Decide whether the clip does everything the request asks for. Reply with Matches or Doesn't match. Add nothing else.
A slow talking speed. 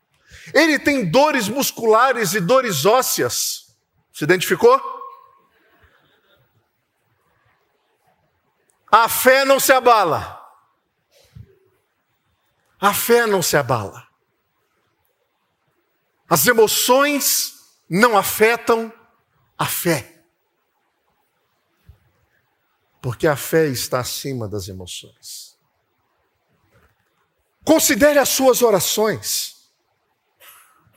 Matches